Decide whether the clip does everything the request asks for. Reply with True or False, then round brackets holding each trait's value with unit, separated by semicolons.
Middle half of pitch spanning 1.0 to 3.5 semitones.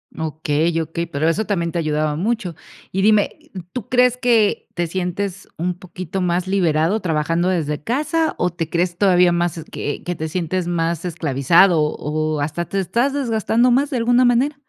False (4.8 semitones)